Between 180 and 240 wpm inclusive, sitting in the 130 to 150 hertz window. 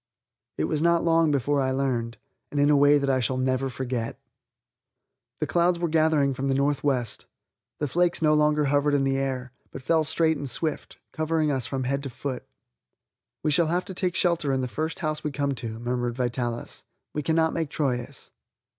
Yes: average, 195 wpm; medium, 140 Hz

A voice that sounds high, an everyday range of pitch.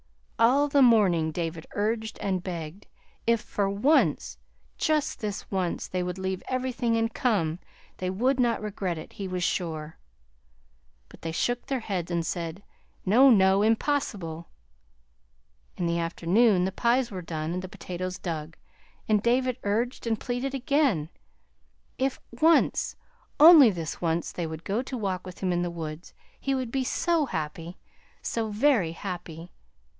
No: high, 195 Hz; wide, 6.0 semitones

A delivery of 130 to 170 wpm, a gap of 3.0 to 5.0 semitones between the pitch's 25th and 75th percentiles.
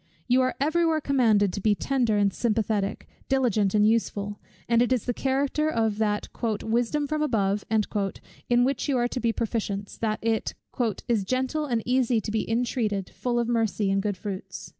No: average, 180 wpm; average, 3.6 semitones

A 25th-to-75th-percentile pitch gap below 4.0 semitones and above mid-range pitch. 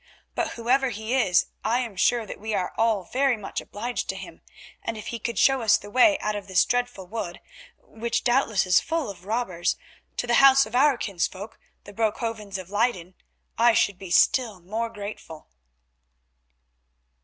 Yes: average, 3.5 semitones; high, 220 Hz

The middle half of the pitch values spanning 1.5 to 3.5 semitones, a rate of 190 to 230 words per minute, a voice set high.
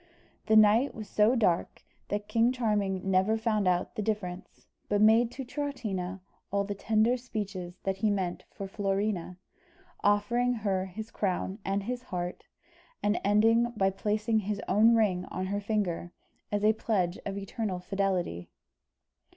No: narrow, 2.5 semitones; average, 150 wpm; high, 205 Hz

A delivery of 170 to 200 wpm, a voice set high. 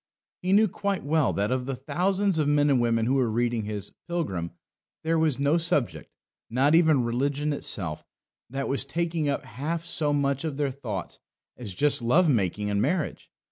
No: average, 180 wpm; medium, 140 Hz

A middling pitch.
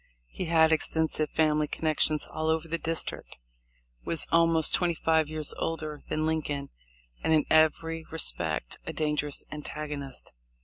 Yes: medium, 155 Hz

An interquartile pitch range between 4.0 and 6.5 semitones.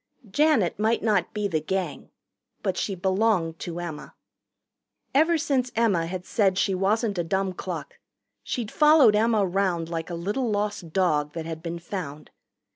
Yes: average, 4.3 semitones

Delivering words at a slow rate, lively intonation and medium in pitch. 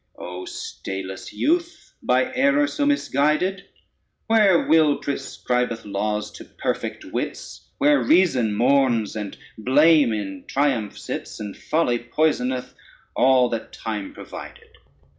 No: slow, 125 wpm; wide, 7.0 semitones; low, 130 Hz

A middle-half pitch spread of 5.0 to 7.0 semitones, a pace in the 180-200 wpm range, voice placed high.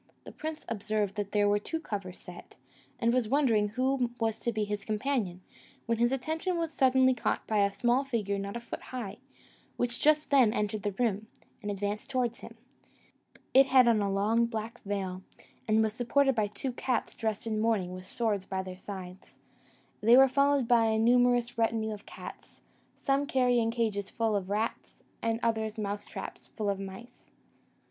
No: average, 3.2 semitones; average, 185 wpm; high, 225 Hz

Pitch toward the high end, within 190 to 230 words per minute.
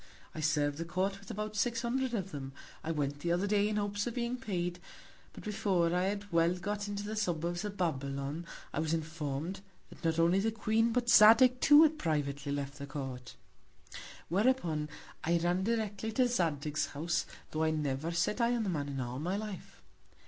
No: medium, 175 Hz; average, 195 wpm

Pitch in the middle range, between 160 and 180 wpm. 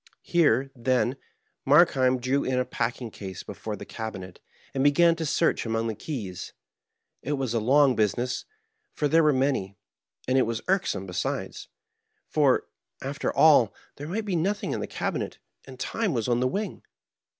No: low, 130 Hz; average, 170 wpm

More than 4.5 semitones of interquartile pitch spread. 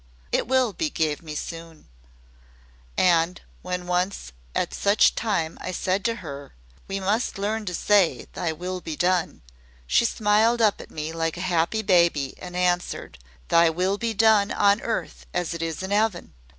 No: average, 3.8 semitones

